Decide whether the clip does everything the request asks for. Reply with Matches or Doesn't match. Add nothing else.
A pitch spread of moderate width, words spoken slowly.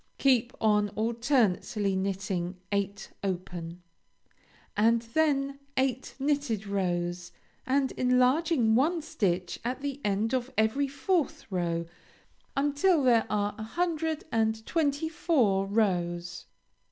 Doesn't match